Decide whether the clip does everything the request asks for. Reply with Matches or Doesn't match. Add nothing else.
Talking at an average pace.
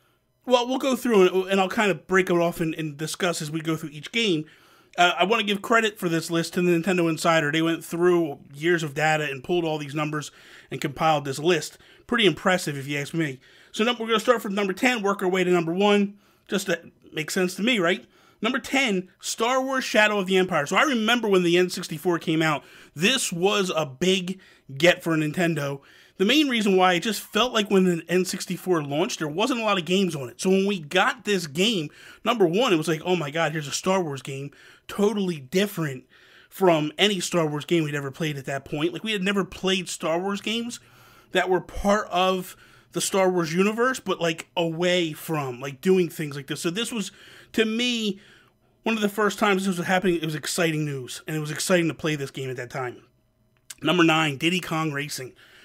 Doesn't match